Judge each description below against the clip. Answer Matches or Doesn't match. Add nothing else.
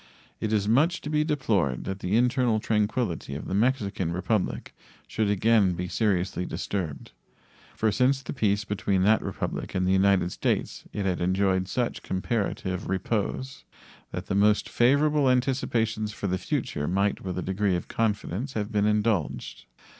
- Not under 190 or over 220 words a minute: Doesn't match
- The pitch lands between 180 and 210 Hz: Doesn't match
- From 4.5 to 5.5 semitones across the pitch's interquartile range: Doesn't match